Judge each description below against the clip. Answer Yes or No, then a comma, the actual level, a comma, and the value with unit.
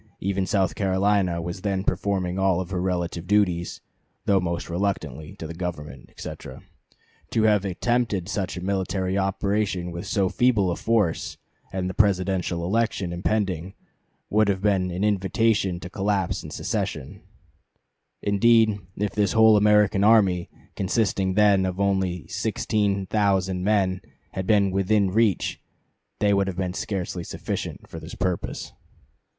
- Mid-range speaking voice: No, very low, 95 Hz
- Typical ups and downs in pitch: No, narrow, 2.2 semitones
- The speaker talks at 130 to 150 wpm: Yes, average, 140 wpm